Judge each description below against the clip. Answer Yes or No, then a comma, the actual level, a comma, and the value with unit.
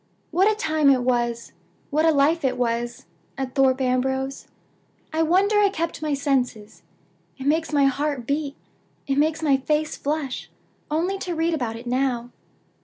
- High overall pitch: Yes, very high, 280 Hz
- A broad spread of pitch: No, average, 3.7 semitones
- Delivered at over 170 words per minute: No, average, 165 wpm